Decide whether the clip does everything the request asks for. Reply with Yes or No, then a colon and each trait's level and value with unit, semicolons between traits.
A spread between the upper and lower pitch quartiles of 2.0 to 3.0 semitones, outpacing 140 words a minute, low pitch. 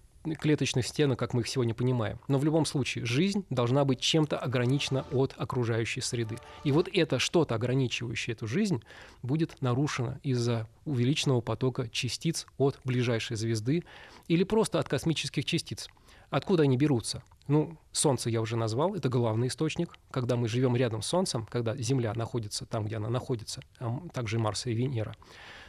No: average, 4.0 semitones; fast, 160 wpm; low, 130 Hz